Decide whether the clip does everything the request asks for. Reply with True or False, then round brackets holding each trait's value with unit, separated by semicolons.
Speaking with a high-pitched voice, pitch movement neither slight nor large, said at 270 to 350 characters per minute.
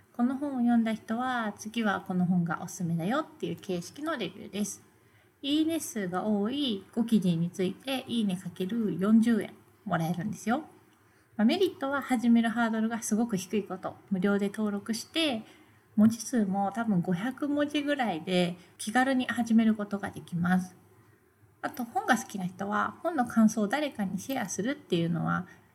True (220 Hz; 4.7 semitones; 330 characters per minute)